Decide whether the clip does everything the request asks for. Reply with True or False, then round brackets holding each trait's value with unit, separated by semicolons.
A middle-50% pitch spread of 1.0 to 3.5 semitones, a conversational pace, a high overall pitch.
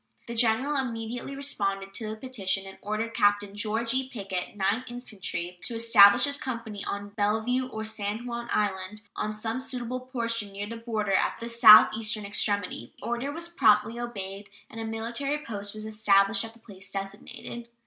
True (2.8 semitones; 170 wpm; 220 Hz)